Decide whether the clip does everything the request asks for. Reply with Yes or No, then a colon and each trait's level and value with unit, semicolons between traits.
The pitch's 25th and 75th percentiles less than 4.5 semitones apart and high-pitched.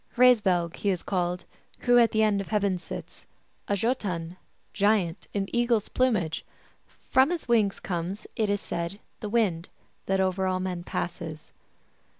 Yes: average, 3.8 semitones; high, 195 Hz